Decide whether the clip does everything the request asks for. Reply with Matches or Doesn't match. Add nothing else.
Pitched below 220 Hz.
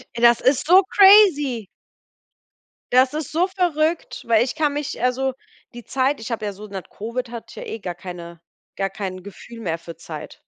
Doesn't match